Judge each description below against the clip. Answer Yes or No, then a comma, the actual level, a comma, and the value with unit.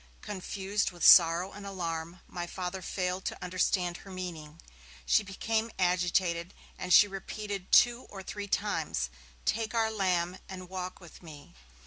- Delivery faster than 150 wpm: No, average, 145 wpm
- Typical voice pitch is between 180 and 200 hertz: Yes, medium, 185 Hz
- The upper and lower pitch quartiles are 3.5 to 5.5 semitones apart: No, narrow, 2.4 semitones